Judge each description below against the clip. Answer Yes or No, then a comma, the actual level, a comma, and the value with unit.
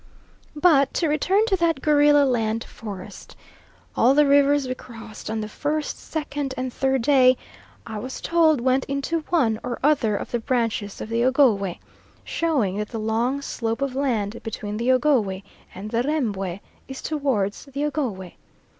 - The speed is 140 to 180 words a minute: Yes, average, 165 wpm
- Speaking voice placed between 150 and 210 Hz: No, very high, 255 Hz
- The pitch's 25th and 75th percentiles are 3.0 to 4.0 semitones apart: No, average, 4.7 semitones